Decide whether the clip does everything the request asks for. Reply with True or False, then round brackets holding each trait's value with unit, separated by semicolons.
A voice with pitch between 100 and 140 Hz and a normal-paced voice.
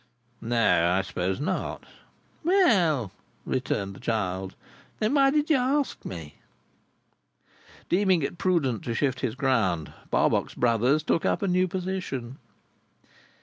False (135 Hz; 125 wpm)